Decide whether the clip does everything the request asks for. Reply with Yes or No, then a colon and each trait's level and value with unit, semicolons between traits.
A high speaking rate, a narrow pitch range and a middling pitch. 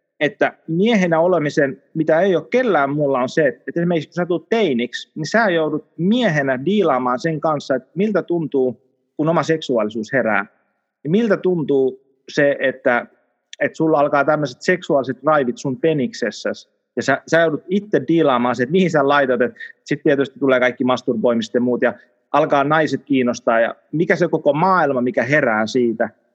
No: fast, 165 wpm; average, 4.4 semitones; medium, 145 Hz